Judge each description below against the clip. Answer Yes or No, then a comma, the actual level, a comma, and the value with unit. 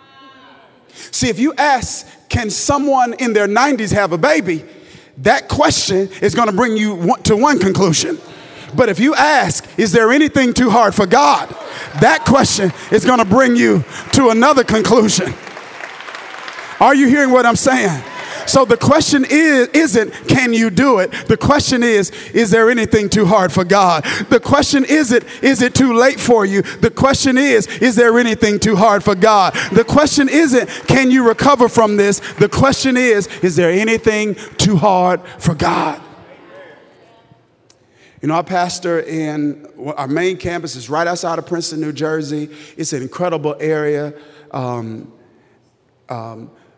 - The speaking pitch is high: Yes, high, 220 Hz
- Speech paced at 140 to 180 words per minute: Yes, average, 160 wpm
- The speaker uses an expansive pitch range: Yes, wide, 6.1 semitones